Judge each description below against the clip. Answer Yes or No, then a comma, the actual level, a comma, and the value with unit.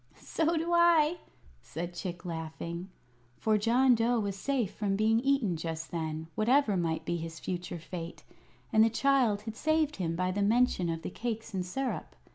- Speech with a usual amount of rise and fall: No, wide, 6.5 semitones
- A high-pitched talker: Yes, high, 205 Hz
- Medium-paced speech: Yes, average, 175 wpm